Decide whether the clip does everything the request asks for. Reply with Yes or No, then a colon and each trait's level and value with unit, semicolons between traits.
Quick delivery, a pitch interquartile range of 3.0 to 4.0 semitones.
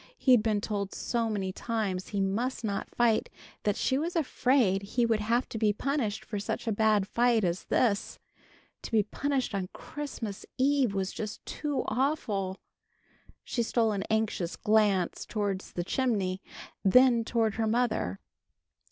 No: average, 155 wpm; average, 3.4 semitones